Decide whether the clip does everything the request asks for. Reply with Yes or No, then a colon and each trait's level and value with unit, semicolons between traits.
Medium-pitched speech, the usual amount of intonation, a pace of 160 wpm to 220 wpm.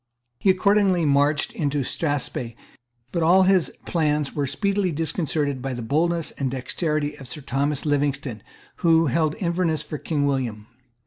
No: medium, 150 Hz; average, 3.4 semitones; average, 145 wpm